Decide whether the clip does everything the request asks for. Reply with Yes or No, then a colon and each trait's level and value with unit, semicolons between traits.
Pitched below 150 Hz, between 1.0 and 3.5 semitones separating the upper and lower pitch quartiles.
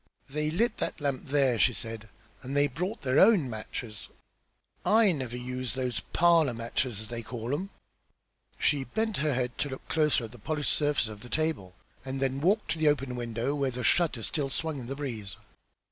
No: low, 135 Hz; average, 4.0 semitones